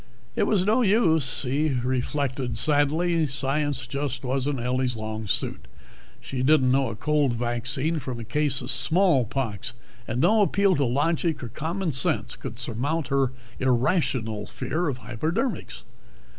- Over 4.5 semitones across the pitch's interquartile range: No, average, 4.2 semitones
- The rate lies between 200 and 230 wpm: No, average, 145 wpm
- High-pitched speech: No, low, 135 Hz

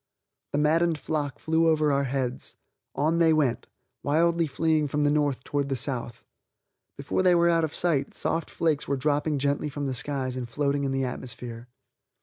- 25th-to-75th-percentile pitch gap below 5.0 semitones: Yes, average, 2.9 semitones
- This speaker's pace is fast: No, average, 180 wpm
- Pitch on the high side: No, medium, 145 Hz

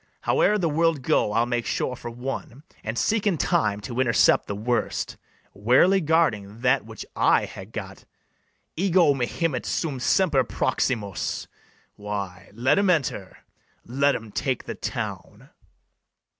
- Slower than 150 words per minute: Yes, average, 140 wpm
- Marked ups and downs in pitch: Yes, wide, 6.2 semitones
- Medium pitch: No, low, 125 Hz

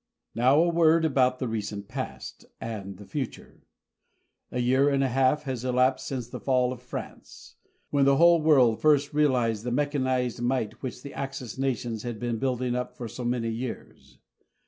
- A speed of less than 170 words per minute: No, average, 175 wpm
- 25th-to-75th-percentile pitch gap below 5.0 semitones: Yes, narrow, 2.4 semitones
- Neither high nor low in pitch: No, low, 130 Hz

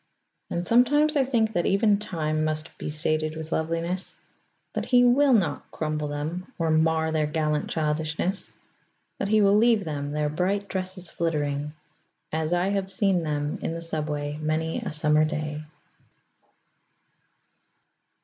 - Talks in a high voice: No, medium, 160 Hz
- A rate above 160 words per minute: No, average, 145 wpm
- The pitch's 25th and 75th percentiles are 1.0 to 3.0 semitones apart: No, average, 4.2 semitones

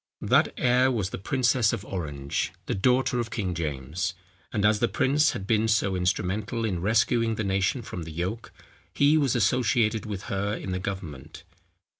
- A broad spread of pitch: No, average, 4.5 semitones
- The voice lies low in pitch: Yes, low, 105 Hz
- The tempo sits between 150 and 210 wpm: Yes, average, 175 wpm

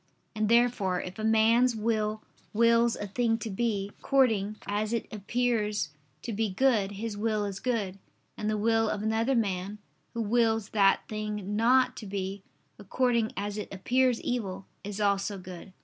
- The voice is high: Yes, high, 215 Hz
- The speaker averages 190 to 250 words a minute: No, average, 165 wpm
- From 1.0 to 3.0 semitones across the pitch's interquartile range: Yes, narrow, 2.4 semitones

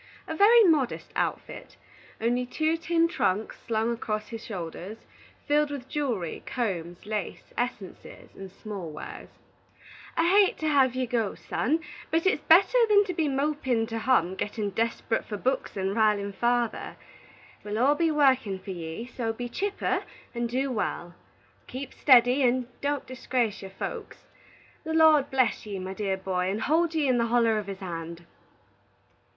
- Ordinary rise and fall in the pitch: No, wide, 6.1 semitones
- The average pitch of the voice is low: No, high, 240 Hz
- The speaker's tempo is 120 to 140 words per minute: No, average, 160 wpm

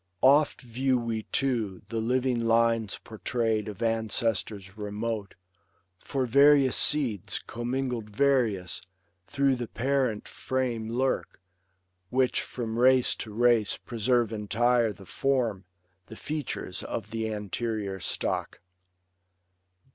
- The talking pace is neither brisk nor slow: No, slow, 110 wpm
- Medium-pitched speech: No, low, 115 Hz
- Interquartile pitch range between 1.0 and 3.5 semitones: Yes, average, 3.2 semitones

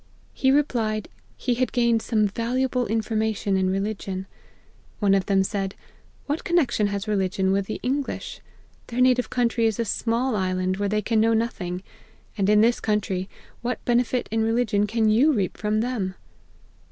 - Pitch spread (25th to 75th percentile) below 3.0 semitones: No, average, 3.4 semitones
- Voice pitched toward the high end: Yes, high, 220 Hz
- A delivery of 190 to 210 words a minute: No, average, 165 wpm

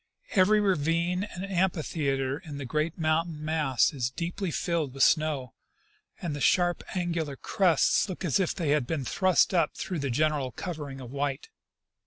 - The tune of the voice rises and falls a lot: No, average, 3.8 semitones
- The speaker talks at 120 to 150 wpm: No, average, 165 wpm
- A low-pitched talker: No, medium, 155 Hz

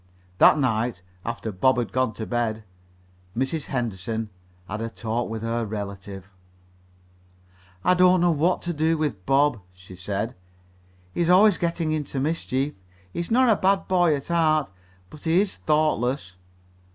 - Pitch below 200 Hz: Yes, low, 135 Hz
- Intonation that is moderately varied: No, wide, 6.8 semitones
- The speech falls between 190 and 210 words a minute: No, average, 155 wpm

